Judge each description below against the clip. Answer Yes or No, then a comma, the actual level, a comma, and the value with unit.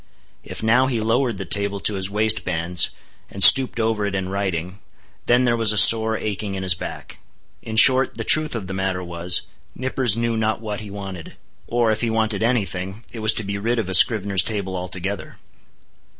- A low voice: Yes, low, 105 Hz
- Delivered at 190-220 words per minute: Yes, average, 200 wpm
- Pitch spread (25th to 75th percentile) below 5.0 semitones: Yes, average, 3.0 semitones